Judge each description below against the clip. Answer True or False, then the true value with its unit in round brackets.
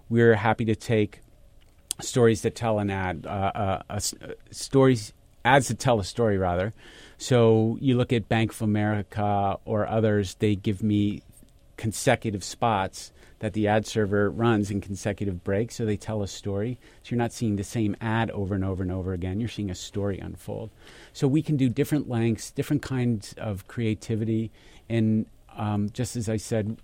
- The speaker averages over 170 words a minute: True (180 wpm)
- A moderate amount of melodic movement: False (2.3 semitones)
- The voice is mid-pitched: False (110 Hz)